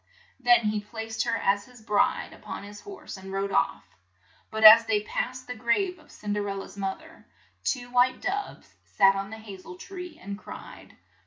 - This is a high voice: Yes, high, 220 Hz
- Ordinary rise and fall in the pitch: Yes, average, 3.7 semitones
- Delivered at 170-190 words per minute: No, average, 200 wpm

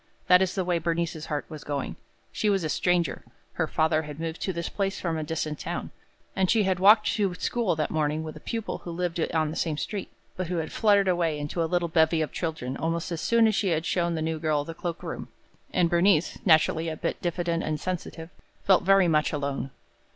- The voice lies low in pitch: No, medium, 170 Hz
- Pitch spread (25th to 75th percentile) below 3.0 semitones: Yes, narrow, 2.6 semitones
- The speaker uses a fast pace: Yes, fast, 225 wpm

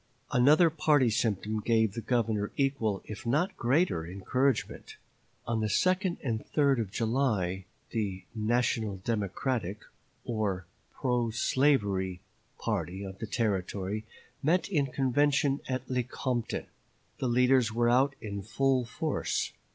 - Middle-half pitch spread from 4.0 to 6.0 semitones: Yes, average, 4.5 semitones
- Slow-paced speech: Yes, slow, 120 wpm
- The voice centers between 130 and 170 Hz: No, low, 120 Hz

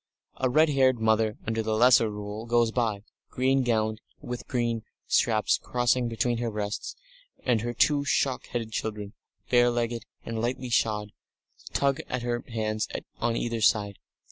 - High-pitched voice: No, low, 115 Hz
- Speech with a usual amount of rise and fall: No, narrow, 2.0 semitones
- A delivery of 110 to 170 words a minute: Yes, average, 160 wpm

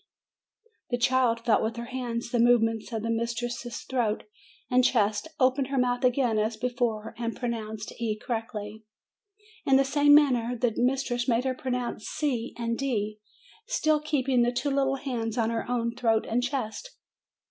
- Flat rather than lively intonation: Yes, narrow, 2.3 semitones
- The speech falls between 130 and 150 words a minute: No, average, 170 wpm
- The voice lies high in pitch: Yes, high, 240 Hz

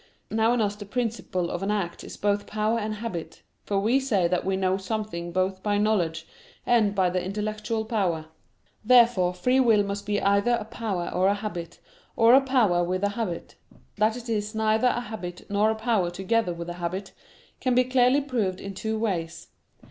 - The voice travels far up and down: No, average, 3.5 semitones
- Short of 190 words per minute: No, average, 195 wpm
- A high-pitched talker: Yes, high, 205 Hz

